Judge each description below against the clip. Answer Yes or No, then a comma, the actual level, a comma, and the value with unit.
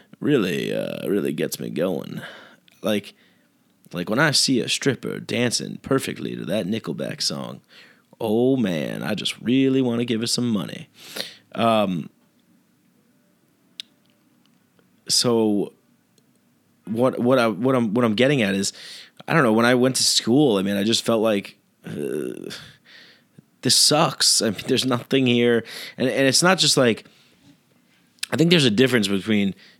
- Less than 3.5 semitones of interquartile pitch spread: Yes, average, 3.0 semitones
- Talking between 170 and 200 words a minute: No, average, 155 wpm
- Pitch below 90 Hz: No, low, 120 Hz